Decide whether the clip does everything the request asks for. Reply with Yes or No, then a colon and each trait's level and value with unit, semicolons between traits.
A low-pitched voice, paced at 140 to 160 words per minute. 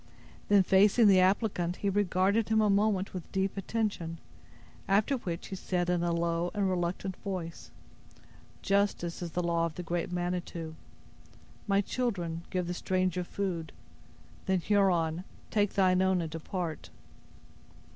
No: medium, 185 Hz; average, 145 wpm